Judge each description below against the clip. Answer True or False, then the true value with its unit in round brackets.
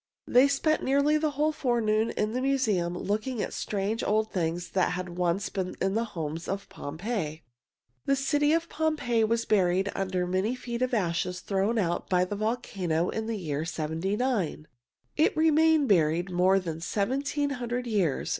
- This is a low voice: False (210 Hz)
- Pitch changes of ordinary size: False (6.0 semitones)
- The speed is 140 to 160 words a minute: False (170 wpm)